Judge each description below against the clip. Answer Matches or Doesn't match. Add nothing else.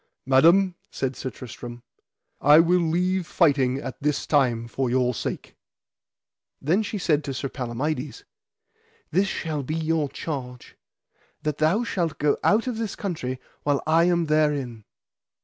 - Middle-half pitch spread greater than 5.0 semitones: Doesn't match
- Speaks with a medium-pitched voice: Matches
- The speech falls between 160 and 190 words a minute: Doesn't match